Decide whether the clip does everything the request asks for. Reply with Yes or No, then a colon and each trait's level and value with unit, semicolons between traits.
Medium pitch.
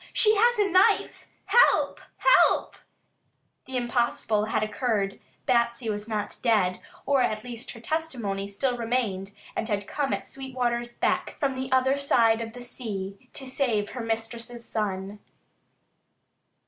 No: high, 235 Hz